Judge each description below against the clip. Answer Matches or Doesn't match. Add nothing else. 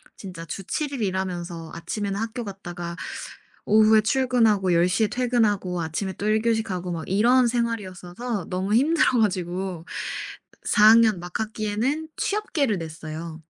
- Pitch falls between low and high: Doesn't match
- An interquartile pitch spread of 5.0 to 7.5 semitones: Doesn't match